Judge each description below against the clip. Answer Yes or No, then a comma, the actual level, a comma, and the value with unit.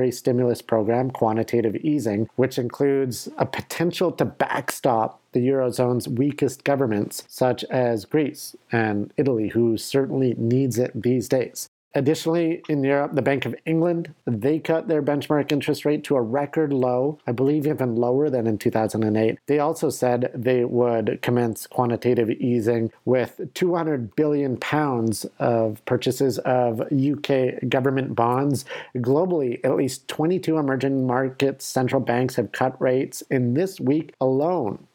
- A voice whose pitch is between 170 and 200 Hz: No, low, 130 Hz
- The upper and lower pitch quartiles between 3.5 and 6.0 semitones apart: No, average, 3.0 semitones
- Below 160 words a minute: Yes, average, 140 wpm